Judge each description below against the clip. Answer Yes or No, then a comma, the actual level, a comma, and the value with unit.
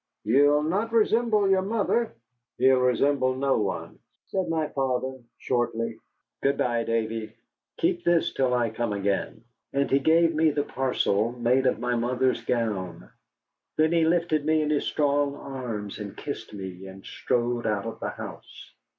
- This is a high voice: No, low, 130 Hz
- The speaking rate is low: No, average, 160 wpm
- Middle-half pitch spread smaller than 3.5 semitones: No, average, 5.1 semitones